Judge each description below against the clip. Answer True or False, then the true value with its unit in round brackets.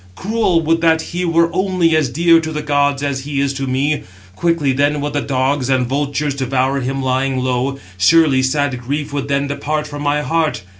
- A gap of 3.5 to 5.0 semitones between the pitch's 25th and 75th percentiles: False (2.8 semitones)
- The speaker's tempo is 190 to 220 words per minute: True (200 wpm)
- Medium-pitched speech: True (145 Hz)